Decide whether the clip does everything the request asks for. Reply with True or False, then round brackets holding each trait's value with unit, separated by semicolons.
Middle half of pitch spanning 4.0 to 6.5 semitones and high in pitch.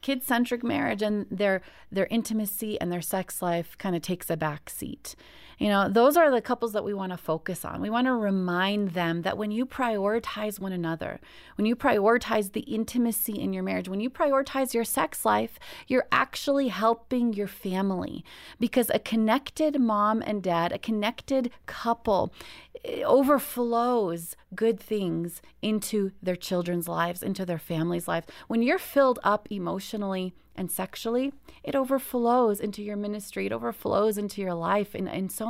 True (4.4 semitones; 210 Hz)